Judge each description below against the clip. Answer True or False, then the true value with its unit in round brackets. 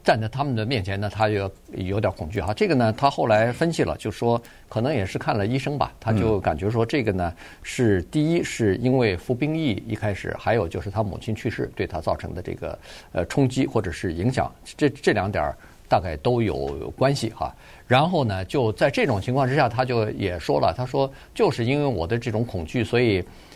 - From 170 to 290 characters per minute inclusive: False (305 characters per minute)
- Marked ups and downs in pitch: False (3.9 semitones)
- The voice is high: False (115 Hz)